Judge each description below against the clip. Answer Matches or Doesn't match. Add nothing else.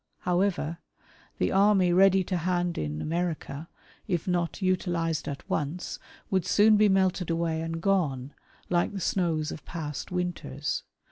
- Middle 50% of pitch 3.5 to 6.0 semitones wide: Doesn't match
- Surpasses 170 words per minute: Doesn't match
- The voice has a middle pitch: Matches